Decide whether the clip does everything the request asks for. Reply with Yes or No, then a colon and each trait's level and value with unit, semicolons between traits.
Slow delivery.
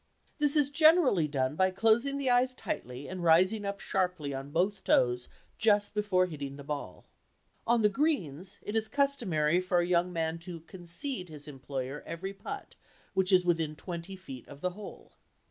No: average, 175 wpm